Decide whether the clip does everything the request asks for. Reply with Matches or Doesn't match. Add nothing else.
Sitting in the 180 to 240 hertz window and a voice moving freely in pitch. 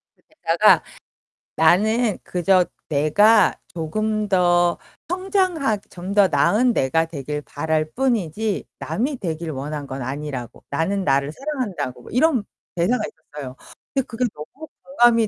Matches